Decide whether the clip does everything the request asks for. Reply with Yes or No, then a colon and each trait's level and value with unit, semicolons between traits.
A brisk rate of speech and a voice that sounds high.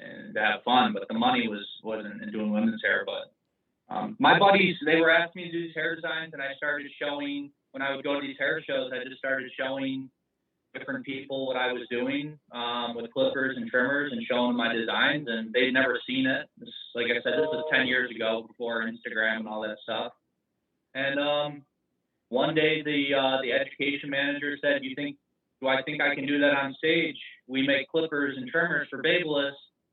No: fast, 215 wpm; medium, 140 Hz